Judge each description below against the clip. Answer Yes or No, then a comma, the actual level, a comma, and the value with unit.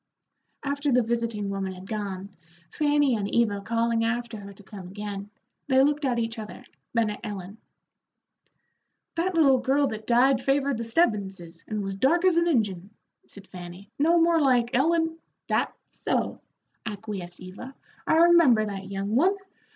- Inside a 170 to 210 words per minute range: No, average, 160 wpm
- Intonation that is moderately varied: No, wide, 5.7 semitones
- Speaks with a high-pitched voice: Yes, high, 230 Hz